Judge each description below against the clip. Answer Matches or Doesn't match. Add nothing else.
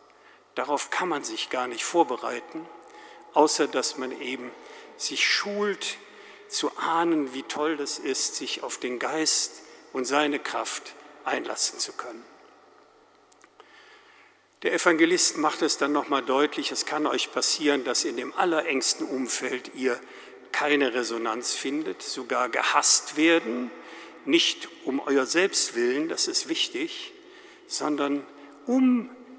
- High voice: Matches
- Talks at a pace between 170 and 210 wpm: Doesn't match